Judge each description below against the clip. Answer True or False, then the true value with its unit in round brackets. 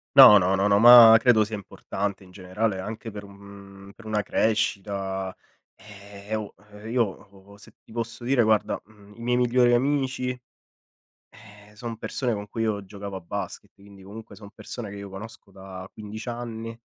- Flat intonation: True (2.3 semitones)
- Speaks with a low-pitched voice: True (105 Hz)